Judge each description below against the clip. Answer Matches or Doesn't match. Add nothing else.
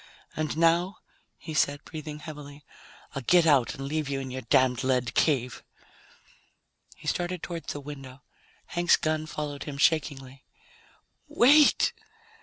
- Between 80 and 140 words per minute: Matches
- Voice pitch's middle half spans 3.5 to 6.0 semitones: Doesn't match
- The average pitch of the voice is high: Doesn't match